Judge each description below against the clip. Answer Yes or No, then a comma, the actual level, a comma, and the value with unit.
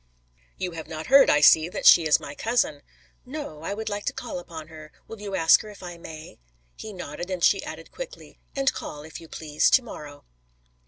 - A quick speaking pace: Yes, fast, 215 wpm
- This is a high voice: No, medium, 170 Hz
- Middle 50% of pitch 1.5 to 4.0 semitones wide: No, wide, 5.5 semitones